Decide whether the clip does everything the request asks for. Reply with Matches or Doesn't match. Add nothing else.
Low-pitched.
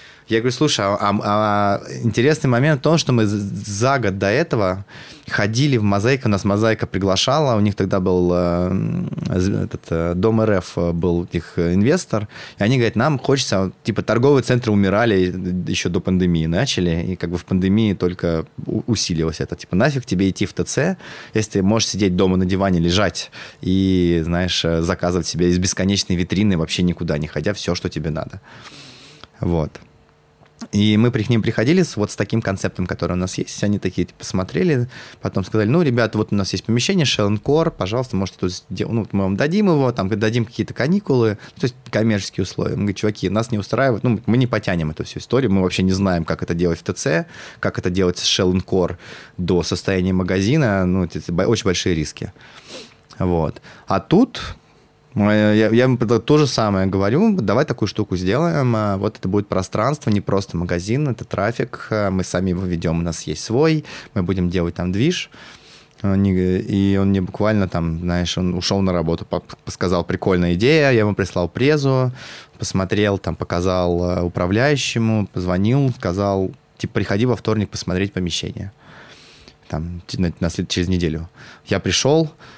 Matches